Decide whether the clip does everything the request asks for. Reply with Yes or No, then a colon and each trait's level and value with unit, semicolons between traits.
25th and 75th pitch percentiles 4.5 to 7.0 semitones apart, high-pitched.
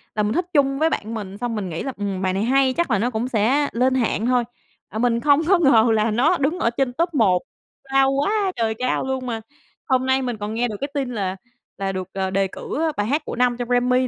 No: average, 4.1 semitones; high, 245 Hz